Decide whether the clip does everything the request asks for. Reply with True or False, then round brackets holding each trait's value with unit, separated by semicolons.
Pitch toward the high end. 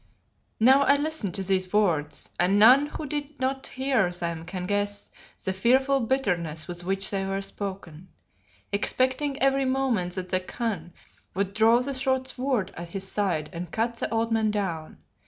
True (205 Hz)